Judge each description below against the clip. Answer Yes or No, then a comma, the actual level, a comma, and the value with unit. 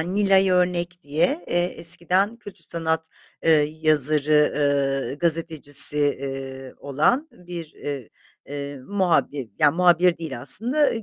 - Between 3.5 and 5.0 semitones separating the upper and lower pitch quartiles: Yes, average, 3.8 semitones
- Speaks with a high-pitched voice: No, medium, 160 Hz